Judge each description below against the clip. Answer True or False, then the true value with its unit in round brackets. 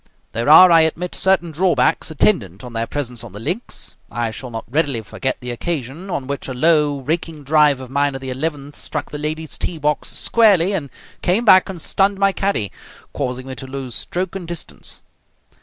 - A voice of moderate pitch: True (150 Hz)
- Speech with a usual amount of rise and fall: True (4.9 semitones)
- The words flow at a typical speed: True (195 wpm)